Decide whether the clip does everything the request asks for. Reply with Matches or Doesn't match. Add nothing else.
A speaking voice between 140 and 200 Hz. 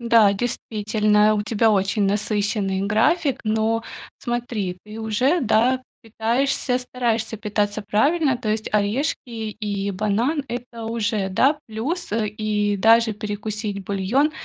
Doesn't match